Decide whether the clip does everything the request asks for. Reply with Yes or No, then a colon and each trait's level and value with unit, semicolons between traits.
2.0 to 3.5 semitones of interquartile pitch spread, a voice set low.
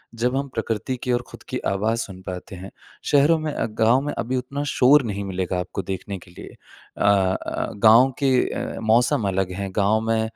No: average, 4.7 semitones; low, 110 Hz